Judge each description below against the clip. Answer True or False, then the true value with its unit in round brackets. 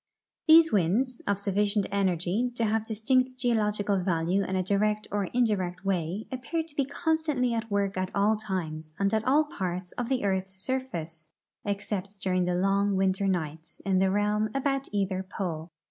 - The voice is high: True (200 Hz)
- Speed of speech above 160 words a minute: True (175 wpm)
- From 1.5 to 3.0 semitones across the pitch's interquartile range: False (3.8 semitones)